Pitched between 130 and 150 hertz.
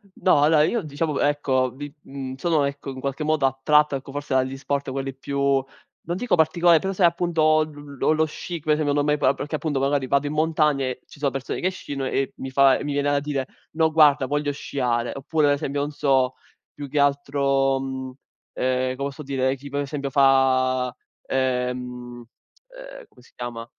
Yes: medium, 140 Hz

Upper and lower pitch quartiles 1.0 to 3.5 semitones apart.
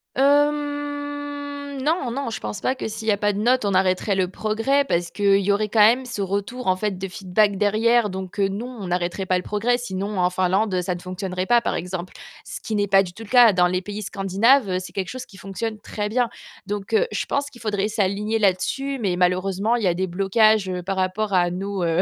No: average, 4.0 semitones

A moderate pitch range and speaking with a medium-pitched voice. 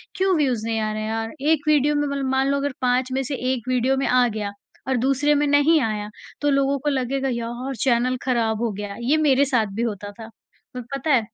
No: average, 3.5 semitones; very high, 255 Hz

